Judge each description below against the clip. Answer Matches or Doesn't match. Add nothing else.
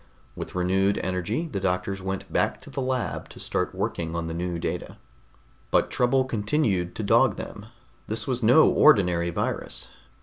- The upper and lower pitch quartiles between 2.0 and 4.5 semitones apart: Doesn't match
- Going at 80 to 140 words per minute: Doesn't match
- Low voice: Matches